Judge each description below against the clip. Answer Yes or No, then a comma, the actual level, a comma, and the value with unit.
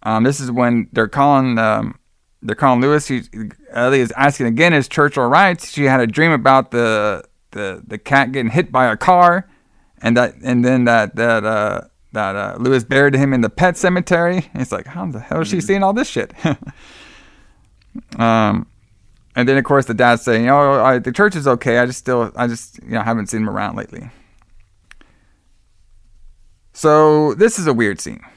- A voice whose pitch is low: Yes, low, 125 Hz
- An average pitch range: Yes, average, 4.4 semitones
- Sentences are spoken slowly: No, average, 200 wpm